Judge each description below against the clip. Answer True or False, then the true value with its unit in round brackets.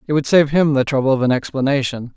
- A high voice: False (140 Hz)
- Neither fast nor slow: False (250 wpm)